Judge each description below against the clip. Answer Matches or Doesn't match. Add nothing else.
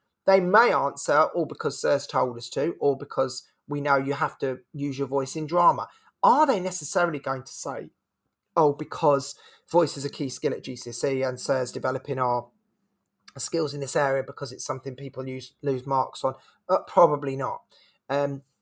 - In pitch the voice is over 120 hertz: Matches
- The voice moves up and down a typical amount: Doesn't match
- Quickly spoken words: Doesn't match